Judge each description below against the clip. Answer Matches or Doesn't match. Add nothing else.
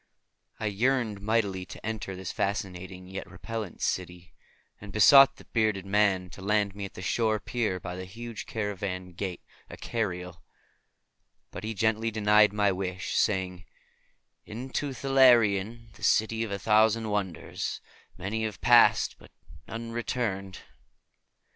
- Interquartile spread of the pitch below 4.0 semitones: Matches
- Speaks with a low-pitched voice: Matches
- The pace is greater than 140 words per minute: Doesn't match